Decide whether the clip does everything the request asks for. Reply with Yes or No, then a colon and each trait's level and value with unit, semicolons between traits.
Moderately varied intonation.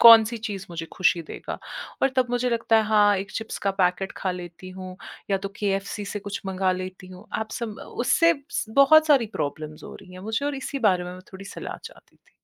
Yes: average, 3.7 semitones